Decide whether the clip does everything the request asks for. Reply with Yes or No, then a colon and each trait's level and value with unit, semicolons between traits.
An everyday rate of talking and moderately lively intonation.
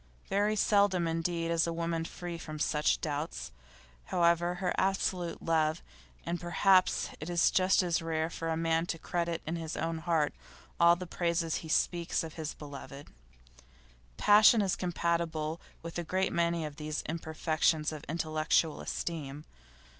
No: average, 150 wpm; narrow, 1.6 semitones